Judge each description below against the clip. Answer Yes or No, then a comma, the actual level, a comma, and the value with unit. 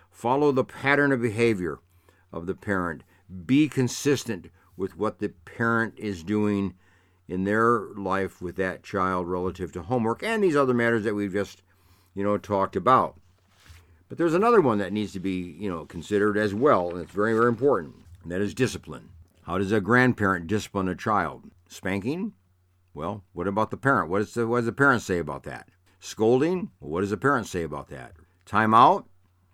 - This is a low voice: Yes, low, 100 Hz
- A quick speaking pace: No, average, 185 wpm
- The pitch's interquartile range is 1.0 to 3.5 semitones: No, average, 4.2 semitones